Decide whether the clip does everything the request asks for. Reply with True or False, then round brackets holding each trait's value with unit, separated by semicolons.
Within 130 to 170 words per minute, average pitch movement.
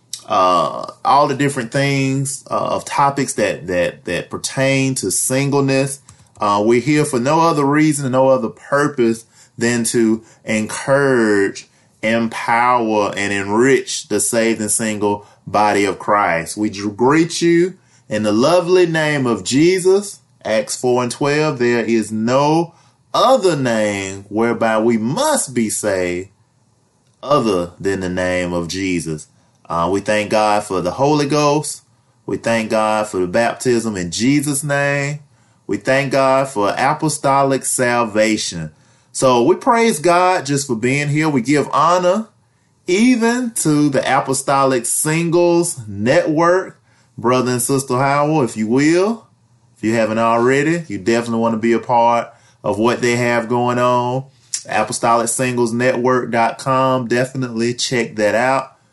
True (140 wpm; 4.0 semitones)